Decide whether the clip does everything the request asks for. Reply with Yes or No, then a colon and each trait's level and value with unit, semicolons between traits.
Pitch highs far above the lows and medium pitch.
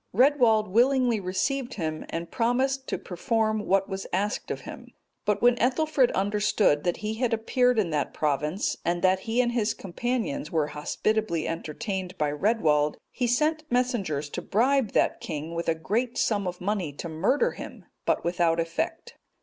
No: wide, 6.3 semitones; high, 210 Hz